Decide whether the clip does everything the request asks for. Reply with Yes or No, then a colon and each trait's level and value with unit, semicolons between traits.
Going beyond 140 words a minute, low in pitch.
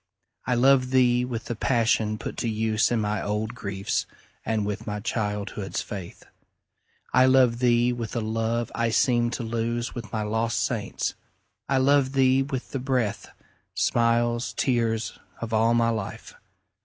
Yes: average, 155 wpm; low, 115 Hz